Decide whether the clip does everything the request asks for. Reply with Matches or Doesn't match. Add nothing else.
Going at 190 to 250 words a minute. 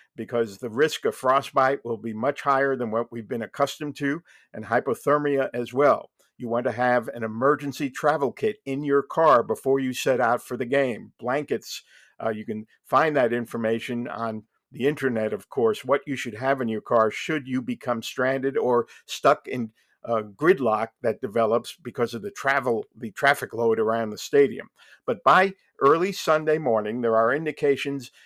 Doesn't match